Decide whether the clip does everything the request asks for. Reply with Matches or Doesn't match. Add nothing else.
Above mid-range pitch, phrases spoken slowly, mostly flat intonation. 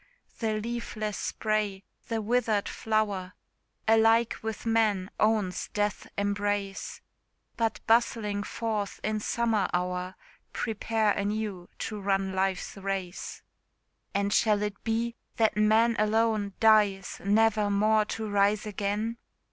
Matches